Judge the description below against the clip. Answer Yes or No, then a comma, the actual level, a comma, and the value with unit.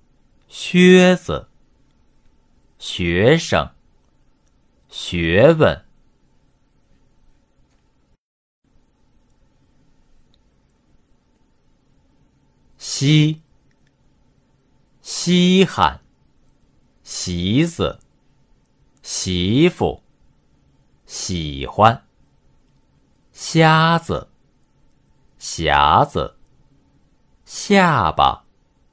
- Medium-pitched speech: No, very low, 95 Hz